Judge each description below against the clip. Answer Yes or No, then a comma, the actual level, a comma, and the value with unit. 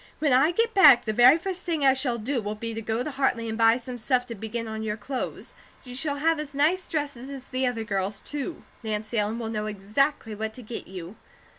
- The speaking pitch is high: Yes, high, 245 Hz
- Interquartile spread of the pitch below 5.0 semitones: Yes, average, 4.5 semitones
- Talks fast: Yes, fast, 240 wpm